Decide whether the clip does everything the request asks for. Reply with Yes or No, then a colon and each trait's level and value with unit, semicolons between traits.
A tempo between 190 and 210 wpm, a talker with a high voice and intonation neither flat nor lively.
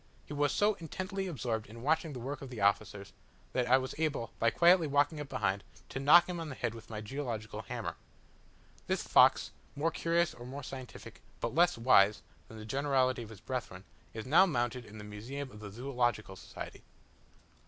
No: average, 195 wpm; low, 130 Hz; average, 4.9 semitones